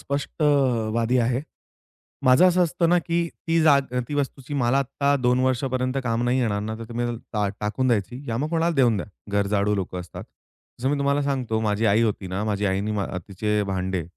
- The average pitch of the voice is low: Yes, low, 120 Hz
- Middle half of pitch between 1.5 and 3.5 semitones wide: No, average, 4.9 semitones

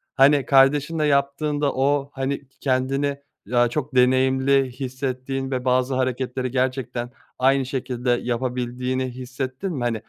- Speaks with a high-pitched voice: No, low, 130 Hz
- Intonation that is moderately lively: No, narrow, 1.5 semitones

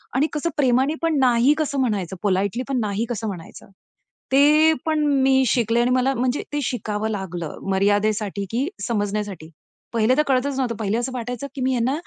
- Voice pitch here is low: No, high, 240 Hz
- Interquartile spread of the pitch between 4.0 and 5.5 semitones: Yes, average, 4.3 semitones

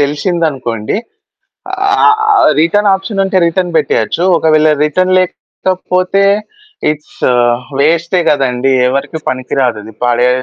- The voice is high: No, medium, 160 Hz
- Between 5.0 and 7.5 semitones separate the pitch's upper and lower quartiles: Yes, wide, 5.5 semitones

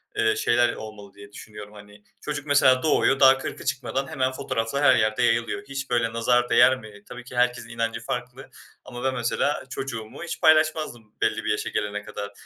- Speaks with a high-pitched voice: No, low, 120 Hz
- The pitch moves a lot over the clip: No, average, 3.4 semitones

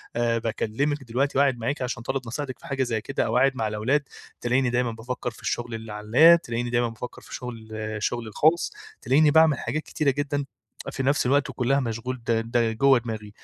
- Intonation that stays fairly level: No, average, 3.2 semitones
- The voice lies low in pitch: Yes, low, 125 Hz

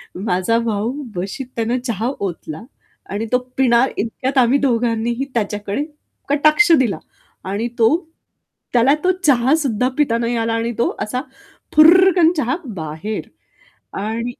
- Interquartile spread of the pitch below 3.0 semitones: No, average, 3.7 semitones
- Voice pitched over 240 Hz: No, high, 235 Hz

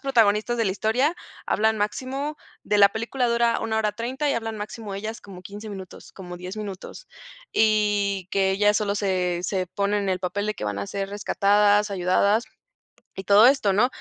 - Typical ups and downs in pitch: No, narrow, 2.2 semitones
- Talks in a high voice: Yes, high, 205 Hz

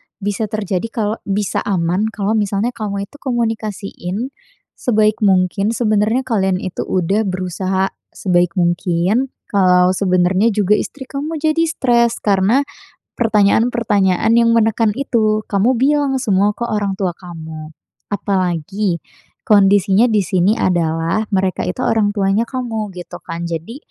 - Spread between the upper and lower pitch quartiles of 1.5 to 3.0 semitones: No, average, 3.4 semitones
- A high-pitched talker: Yes, high, 205 Hz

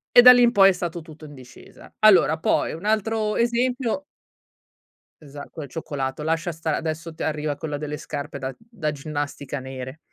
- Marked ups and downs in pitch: Yes, wide, 6.5 semitones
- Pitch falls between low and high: Yes, medium, 160 Hz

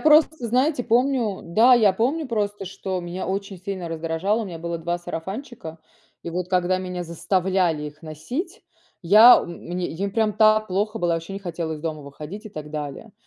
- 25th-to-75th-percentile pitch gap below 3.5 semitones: No, average, 4.4 semitones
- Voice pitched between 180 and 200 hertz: Yes, medium, 185 Hz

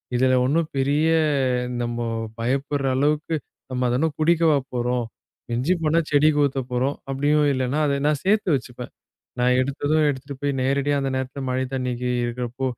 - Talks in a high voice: No, low, 135 Hz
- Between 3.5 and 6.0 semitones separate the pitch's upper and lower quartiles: No, average, 2.8 semitones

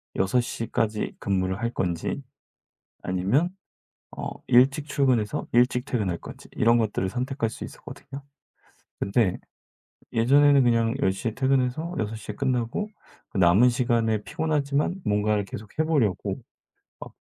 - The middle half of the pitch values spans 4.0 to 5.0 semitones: Yes, average, 4.5 semitones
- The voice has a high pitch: No, low, 115 Hz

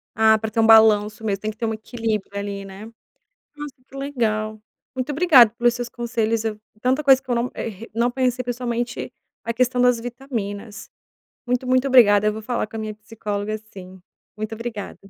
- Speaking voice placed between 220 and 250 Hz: Yes, high, 225 Hz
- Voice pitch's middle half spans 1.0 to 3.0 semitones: Yes, narrow, 2.6 semitones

